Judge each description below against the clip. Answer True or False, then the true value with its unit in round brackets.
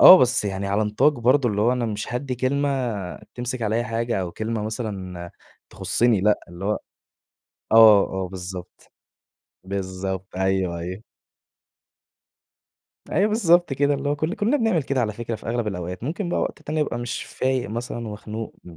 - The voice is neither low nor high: False (115 Hz)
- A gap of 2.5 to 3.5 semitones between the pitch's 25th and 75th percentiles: False (5.0 semitones)